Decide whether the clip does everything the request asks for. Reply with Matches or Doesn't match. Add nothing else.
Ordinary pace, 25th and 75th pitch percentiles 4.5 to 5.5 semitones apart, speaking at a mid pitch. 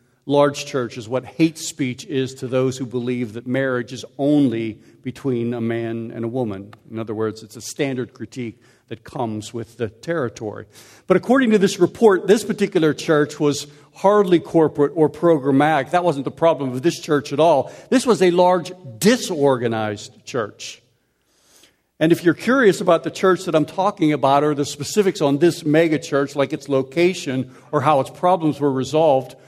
Matches